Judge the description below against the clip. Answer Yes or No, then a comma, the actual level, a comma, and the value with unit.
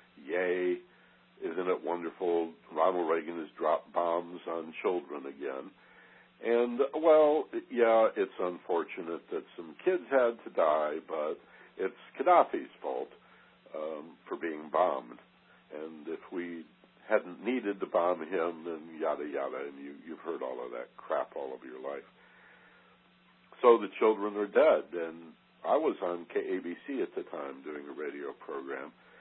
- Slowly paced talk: No, average, 145 wpm